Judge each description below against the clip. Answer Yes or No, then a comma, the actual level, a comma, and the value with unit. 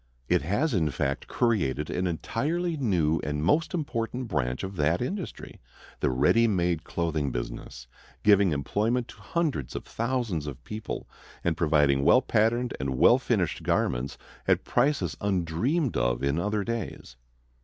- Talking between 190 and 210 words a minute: No, average, 145 wpm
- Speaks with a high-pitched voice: No, very low, 95 Hz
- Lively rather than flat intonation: Yes, wide, 8.2 semitones